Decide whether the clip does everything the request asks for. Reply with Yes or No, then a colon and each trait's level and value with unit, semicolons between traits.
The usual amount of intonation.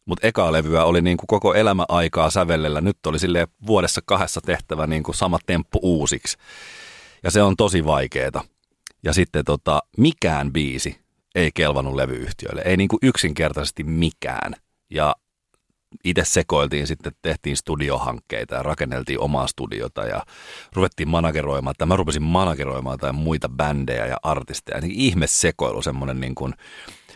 Yes: average, 3.5 semitones